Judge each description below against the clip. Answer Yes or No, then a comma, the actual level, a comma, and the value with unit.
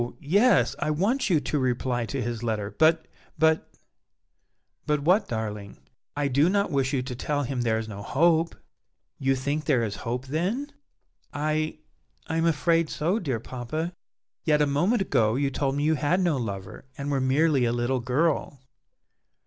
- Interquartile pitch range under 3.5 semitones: No, average, 4.6 semitones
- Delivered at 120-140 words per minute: No, average, 175 wpm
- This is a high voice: No, medium, 145 Hz